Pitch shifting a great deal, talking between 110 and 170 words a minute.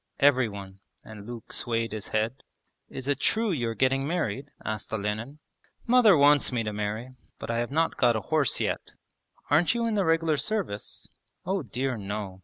No: wide, 6.3 semitones; average, 185 wpm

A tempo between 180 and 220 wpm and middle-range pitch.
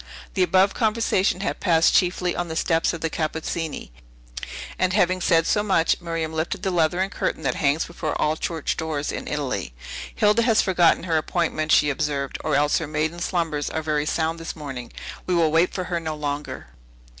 Yes: average, 190 wpm; medium, 165 Hz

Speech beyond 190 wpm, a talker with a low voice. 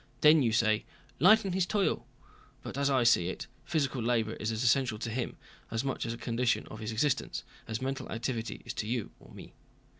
Yes: average, 200 wpm; low, 120 Hz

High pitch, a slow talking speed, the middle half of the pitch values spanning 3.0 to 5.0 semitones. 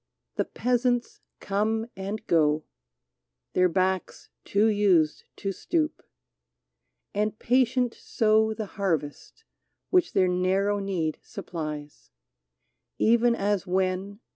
Yes: high, 200 Hz; slow, 110 wpm; average, 3.3 semitones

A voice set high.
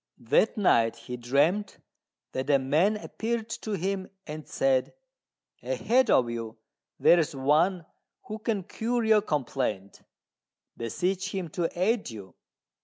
No: medium, 170 Hz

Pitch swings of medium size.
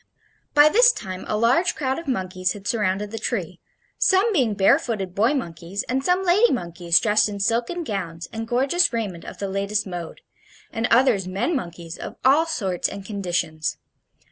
No: wide, 6.3 semitones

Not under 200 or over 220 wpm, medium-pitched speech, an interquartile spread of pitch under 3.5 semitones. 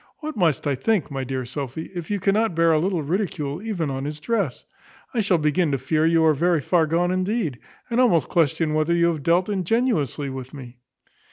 No: fast, 205 wpm; medium, 165 Hz; average, 4.5 semitones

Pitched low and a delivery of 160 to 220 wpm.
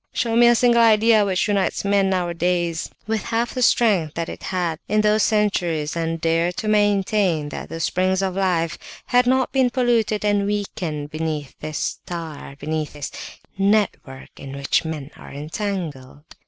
No: medium, 185 Hz; average, 165 wpm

